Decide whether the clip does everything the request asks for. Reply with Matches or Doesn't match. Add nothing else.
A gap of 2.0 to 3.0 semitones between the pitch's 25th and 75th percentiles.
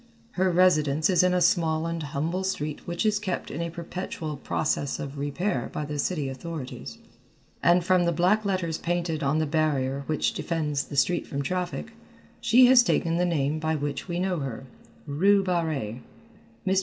Doesn't match